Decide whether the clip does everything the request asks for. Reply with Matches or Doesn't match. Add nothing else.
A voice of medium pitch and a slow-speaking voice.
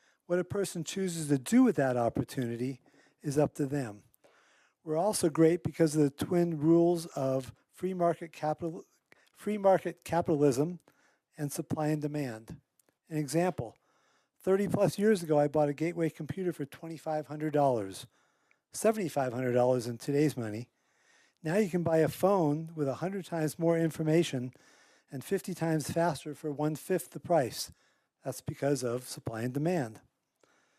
Doesn't match